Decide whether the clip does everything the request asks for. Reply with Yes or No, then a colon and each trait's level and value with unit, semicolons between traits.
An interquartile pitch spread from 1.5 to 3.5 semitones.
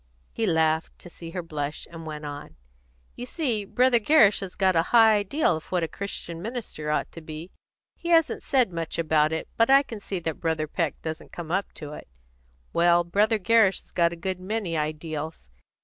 No: average, 5.1 semitones